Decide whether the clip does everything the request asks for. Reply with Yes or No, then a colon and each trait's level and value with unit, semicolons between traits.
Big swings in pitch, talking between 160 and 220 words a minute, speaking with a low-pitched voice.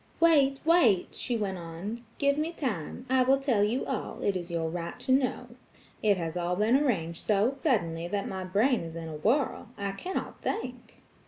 No: wide, 7.1 semitones; average, 185 wpm; high, 215 Hz